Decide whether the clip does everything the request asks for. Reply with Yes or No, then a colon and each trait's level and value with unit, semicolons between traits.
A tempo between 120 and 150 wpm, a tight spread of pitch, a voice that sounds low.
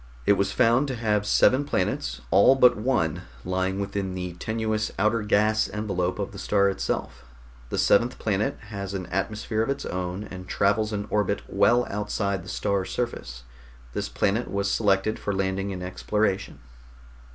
No: average, 165 wpm; narrow, 2.2 semitones; low, 100 Hz